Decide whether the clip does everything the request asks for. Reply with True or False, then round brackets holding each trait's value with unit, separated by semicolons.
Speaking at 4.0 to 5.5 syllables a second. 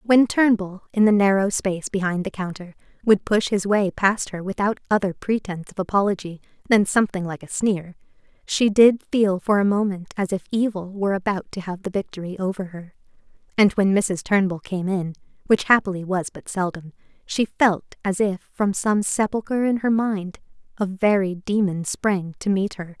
True (5.0 syllables/s)